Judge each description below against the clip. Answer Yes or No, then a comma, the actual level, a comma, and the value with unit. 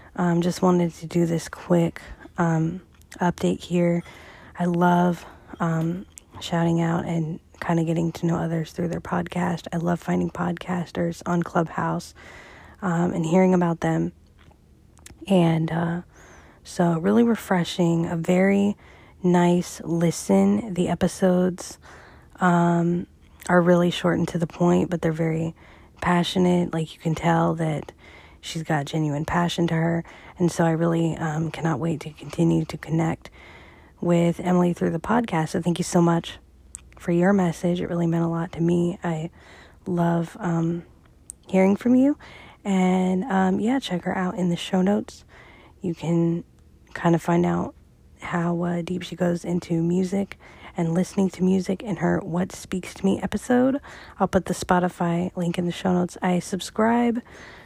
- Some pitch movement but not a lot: No, narrow, 1.5 semitones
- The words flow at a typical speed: Yes, average, 160 wpm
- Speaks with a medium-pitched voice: Yes, medium, 175 Hz